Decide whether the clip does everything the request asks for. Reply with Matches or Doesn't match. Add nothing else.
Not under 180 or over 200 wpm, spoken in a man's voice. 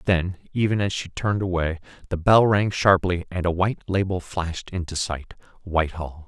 Doesn't match